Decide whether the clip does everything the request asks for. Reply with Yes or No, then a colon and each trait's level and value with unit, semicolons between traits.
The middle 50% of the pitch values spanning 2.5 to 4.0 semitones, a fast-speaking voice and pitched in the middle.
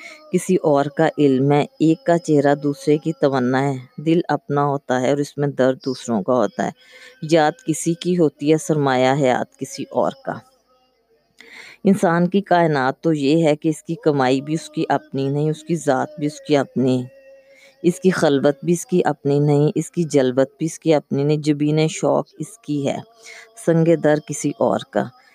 Yes: average, 3.1 semitones; fast, 200 wpm; medium, 155 Hz